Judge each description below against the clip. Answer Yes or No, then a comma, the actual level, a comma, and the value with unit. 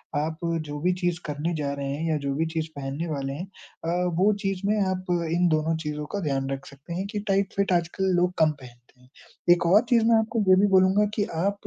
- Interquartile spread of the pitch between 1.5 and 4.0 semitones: No, average, 4.6 semitones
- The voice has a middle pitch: Yes, medium, 170 Hz